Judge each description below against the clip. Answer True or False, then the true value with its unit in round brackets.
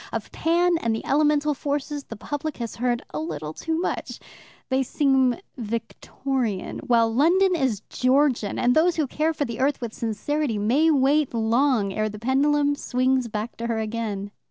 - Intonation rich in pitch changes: False (4.6 semitones)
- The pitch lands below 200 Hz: False (260 Hz)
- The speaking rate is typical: True (170 wpm)